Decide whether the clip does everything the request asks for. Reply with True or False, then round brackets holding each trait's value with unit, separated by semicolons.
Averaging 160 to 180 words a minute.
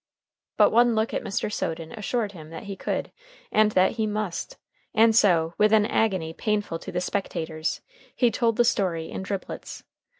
True (175 wpm)